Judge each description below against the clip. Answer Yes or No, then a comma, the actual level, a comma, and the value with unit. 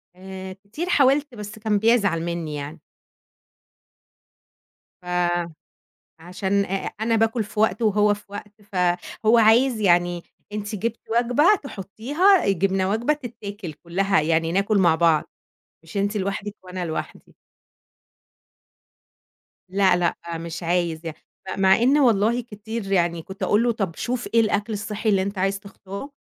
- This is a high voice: Yes, high, 200 Hz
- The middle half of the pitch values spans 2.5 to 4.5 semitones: Yes, average, 3.6 semitones